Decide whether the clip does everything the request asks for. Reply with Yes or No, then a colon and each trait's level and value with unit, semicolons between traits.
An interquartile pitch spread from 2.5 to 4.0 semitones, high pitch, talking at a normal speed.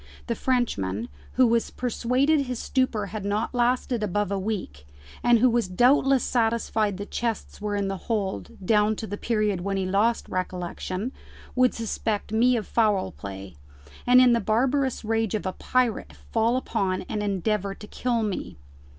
Yes: average, 3.5 semitones; high, 220 Hz; average, 170 wpm